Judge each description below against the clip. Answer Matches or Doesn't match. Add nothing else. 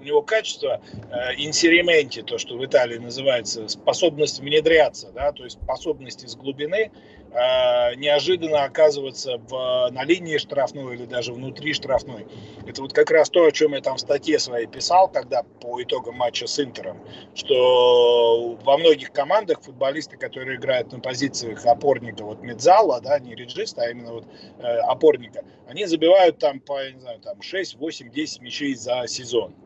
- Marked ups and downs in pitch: Matches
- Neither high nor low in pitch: Matches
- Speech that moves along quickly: Matches